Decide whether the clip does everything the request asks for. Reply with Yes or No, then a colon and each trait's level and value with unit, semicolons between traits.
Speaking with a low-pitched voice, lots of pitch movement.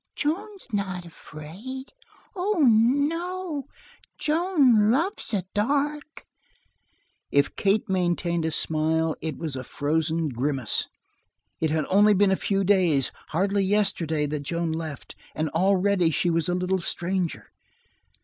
No: medium, 185 Hz; wide, 7.1 semitones